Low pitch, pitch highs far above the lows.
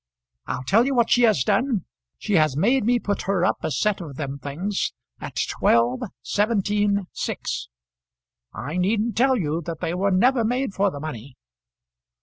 No: high, 195 Hz; wide, 6.3 semitones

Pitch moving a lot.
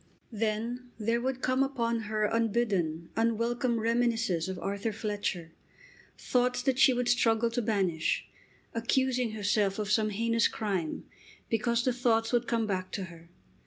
No: average, 2.8 semitones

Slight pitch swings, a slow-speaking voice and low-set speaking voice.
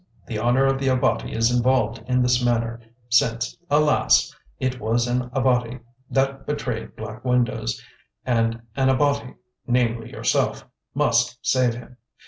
Yes: narrow, 2.0 semitones; slow, 125 wpm; low, 125 Hz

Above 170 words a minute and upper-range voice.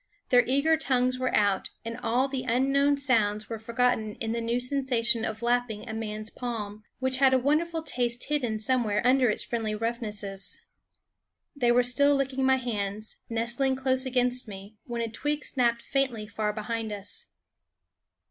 No: average, 165 wpm; high, 240 Hz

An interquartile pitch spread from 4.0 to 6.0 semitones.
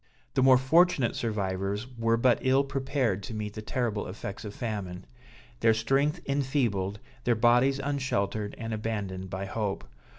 Yes: average, 4.4 semitones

